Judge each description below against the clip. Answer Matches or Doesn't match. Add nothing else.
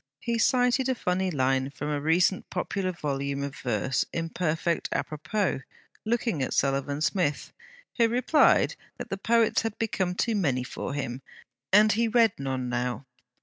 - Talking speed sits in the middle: Matches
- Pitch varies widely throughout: Matches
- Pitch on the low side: Doesn't match